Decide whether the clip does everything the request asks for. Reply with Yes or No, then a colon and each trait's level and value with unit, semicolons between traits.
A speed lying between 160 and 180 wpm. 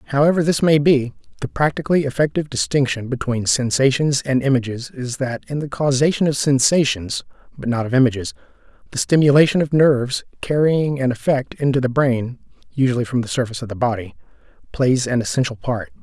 Yes: average, 165 wpm